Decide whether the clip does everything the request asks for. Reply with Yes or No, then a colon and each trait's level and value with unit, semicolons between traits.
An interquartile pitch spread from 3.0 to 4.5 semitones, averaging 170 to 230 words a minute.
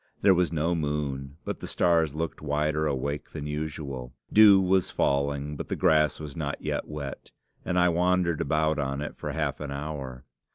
No: narrow, 2.5 semitones; average, 180 wpm